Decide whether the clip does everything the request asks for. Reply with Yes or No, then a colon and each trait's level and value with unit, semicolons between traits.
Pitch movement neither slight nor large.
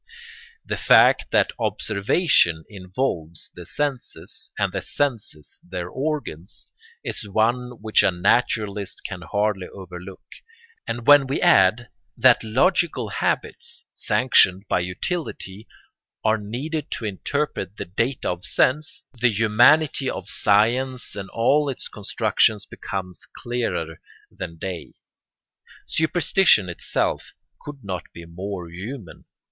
No: wide, 5.7 semitones